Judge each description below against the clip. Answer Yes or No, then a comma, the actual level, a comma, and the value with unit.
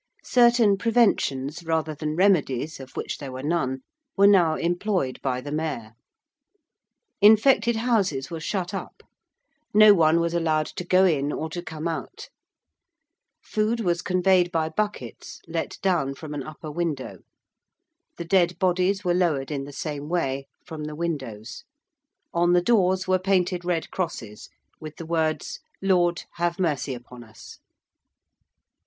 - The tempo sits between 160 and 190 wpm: No, average, 145 wpm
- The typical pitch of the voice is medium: Yes, medium, 170 Hz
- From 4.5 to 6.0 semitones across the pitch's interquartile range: No, average, 3.9 semitones